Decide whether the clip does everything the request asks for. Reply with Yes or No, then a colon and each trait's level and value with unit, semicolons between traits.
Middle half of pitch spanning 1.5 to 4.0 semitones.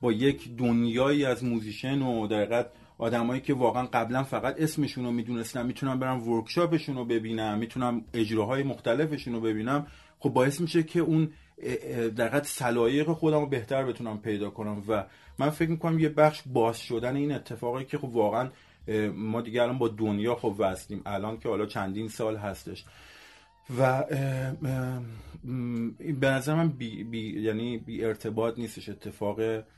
Yes: average, 3.4 semitones